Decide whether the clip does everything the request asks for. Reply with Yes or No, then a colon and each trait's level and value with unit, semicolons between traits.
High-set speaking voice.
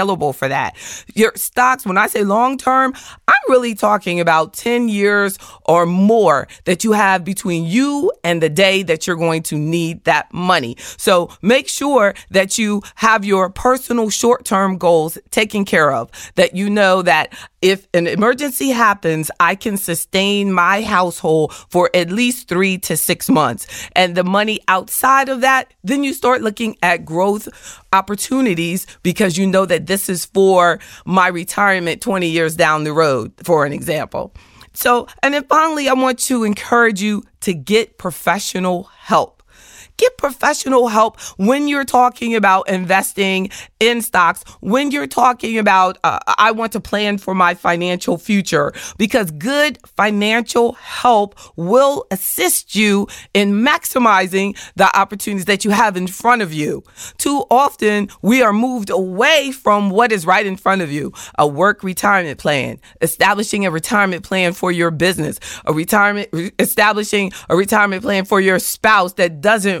Yes: high, 200 Hz